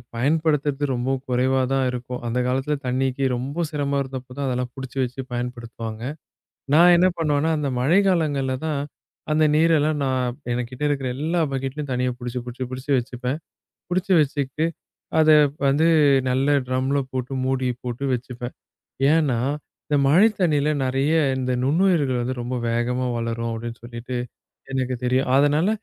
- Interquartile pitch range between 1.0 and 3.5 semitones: Yes, average, 2.9 semitones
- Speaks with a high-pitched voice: No, low, 130 Hz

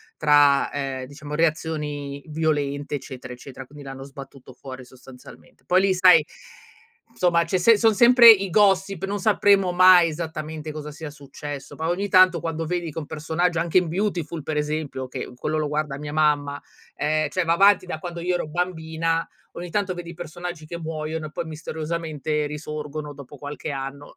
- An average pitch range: Yes, average, 3.2 semitones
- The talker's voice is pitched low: No, medium, 155 Hz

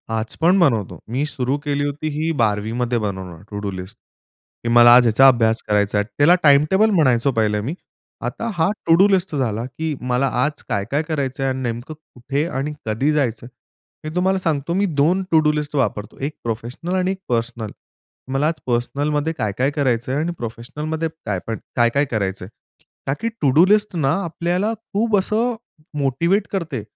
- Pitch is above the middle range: No, medium, 140 Hz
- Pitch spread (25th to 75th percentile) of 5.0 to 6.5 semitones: Yes, wide, 5.6 semitones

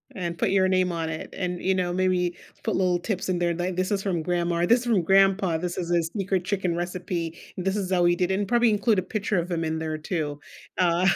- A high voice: No, medium, 180 Hz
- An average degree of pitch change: No, narrow, 1.9 semitones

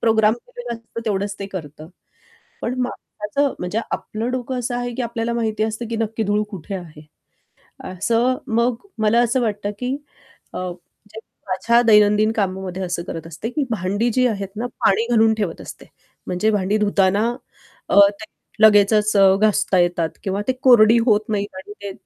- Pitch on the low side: No, high, 215 Hz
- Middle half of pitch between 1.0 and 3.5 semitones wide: Yes, average, 3.0 semitones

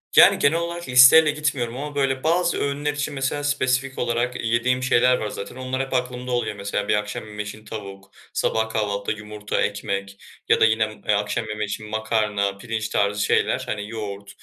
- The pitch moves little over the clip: No, average, 4.0 semitones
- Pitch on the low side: Yes, low, 115 Hz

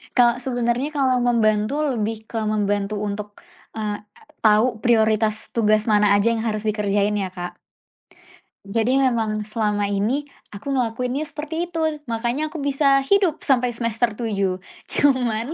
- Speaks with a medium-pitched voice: No, high, 225 Hz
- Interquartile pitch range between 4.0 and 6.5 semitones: No, average, 3.1 semitones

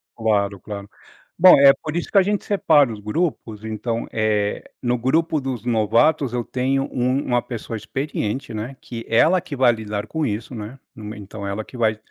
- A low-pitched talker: Yes, low, 120 Hz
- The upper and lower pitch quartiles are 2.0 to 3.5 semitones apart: No, average, 4.3 semitones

